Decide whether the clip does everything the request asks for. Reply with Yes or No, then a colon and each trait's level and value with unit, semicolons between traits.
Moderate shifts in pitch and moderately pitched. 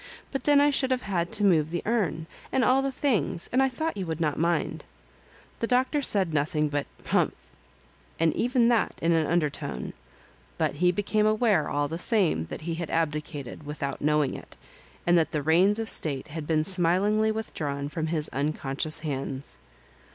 No: wide, 6.2 semitones; medium, 165 Hz